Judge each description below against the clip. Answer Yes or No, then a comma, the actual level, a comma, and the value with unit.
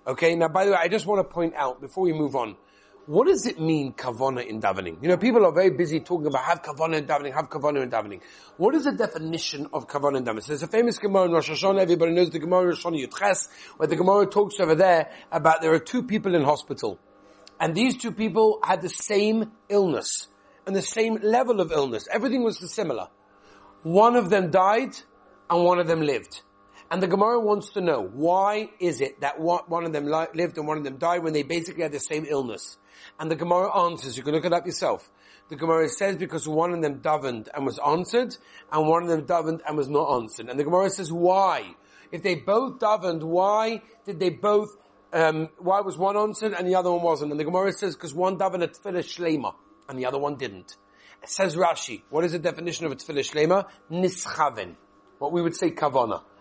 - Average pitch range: Yes, average, 4.1 semitones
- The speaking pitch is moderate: Yes, medium, 170 Hz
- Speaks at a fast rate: Yes, fast, 225 wpm